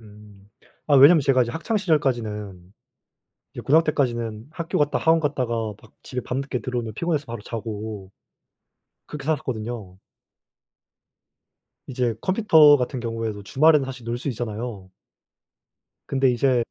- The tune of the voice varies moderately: Yes, average, 4.6 semitones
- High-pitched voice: No, low, 125 Hz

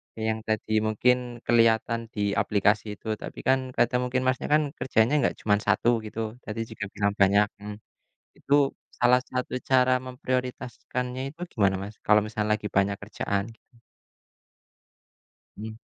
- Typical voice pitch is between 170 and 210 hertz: No, low, 110 Hz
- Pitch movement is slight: No, average, 3.1 semitones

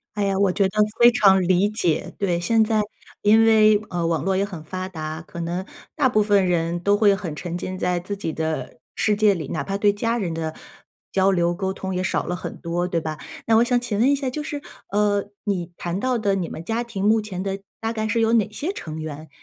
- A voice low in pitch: No, high, 195 Hz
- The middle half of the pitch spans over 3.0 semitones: Yes, average, 3.7 semitones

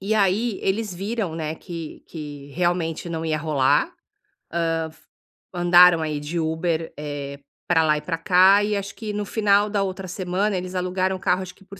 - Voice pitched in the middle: Yes, medium, 180 Hz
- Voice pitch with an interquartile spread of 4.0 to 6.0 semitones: No, average, 3.5 semitones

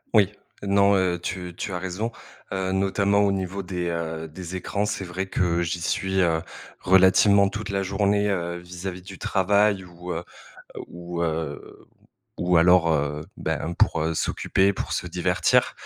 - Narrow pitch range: Yes, narrow, 2.3 semitones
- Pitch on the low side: Yes, very low, 95 Hz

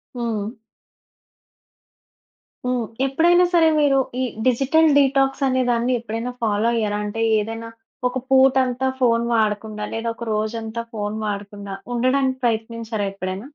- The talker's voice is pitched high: Yes, high, 230 Hz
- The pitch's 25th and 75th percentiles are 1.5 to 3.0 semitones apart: No, average, 3.4 semitones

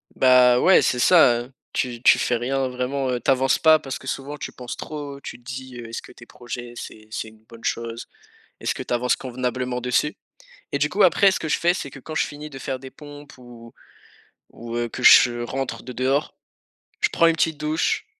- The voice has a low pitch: Yes, low, 130 Hz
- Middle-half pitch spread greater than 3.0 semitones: No, average, 2.7 semitones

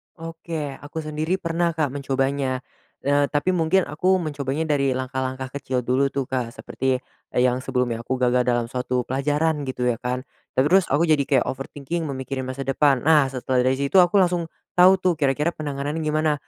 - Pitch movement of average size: Yes, average, 3.5 semitones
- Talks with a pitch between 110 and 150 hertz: Yes, medium, 140 Hz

